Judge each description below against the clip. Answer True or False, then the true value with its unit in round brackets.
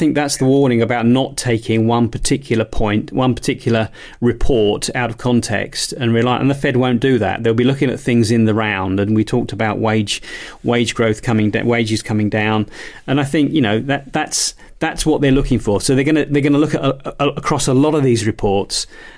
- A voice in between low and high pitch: False (120 Hz)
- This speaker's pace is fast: True (225 wpm)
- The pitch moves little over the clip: False (3.8 semitones)